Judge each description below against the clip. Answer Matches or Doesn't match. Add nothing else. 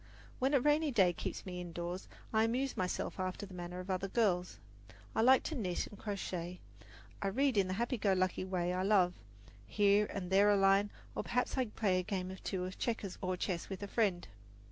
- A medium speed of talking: Doesn't match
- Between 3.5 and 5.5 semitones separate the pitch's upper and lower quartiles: Doesn't match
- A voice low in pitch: Doesn't match